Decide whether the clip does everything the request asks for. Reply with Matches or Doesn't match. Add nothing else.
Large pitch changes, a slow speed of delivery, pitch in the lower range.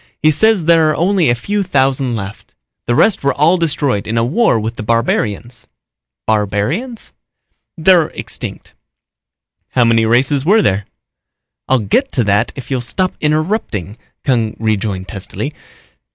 Doesn't match